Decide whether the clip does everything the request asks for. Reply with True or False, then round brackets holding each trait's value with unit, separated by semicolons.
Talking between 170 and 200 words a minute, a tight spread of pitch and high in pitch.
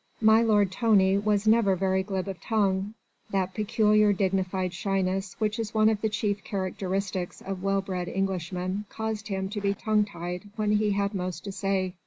True (180 wpm; 1.9 semitones; 195 Hz)